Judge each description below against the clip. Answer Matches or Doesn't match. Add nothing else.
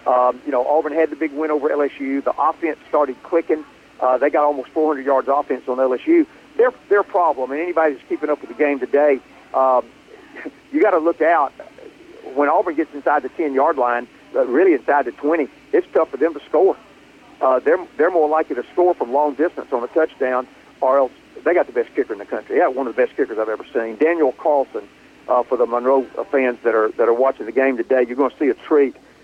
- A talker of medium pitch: Matches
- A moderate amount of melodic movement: Doesn't match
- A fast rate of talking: Matches